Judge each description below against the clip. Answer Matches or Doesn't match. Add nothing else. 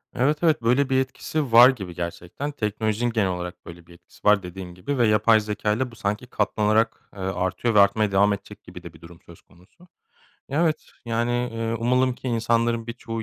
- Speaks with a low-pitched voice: Matches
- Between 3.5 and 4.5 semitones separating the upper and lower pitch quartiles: Matches